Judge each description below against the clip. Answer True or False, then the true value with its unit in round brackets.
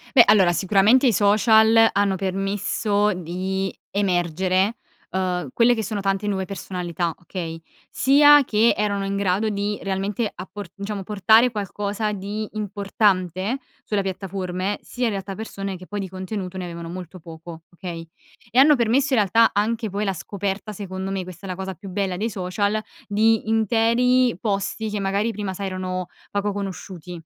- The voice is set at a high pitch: True (200 Hz)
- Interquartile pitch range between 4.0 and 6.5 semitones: False (2.4 semitones)